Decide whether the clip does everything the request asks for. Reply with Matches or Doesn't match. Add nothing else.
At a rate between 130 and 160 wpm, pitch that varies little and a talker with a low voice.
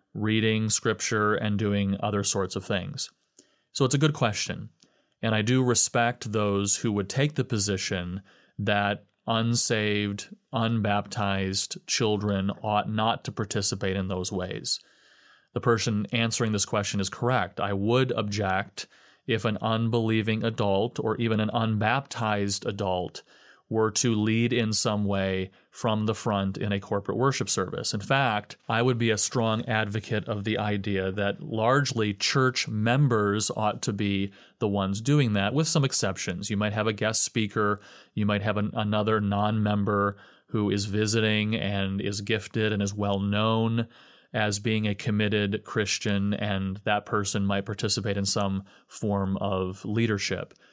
Matches